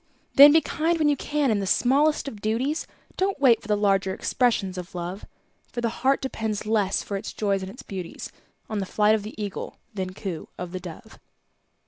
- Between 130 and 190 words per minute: No, fast, 205 wpm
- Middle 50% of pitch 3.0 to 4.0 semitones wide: No, wide, 5.6 semitones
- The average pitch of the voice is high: Yes, high, 215 Hz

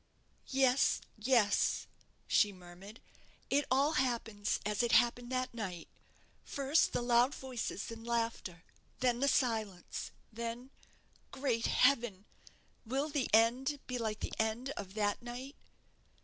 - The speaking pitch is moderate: No, high, 235 Hz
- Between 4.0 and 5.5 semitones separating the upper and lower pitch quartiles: No, average, 3.2 semitones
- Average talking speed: No, slow, 125 wpm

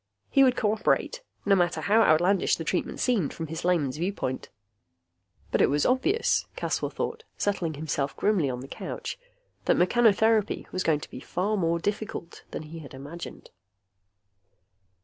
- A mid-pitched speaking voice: Yes, medium, 180 Hz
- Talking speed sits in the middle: Yes, average, 155 wpm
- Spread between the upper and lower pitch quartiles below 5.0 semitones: No, wide, 5.4 semitones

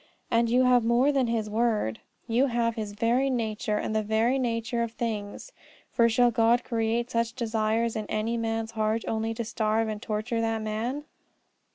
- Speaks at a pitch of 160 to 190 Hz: No, high, 230 Hz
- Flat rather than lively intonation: Yes, narrow, 1.5 semitones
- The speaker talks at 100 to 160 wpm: No, average, 180 wpm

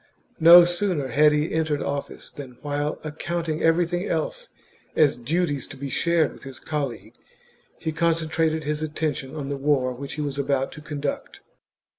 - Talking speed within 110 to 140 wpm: No, average, 165 wpm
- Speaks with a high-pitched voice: No, medium, 150 Hz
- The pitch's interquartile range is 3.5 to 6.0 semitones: No, narrow, 2.5 semitones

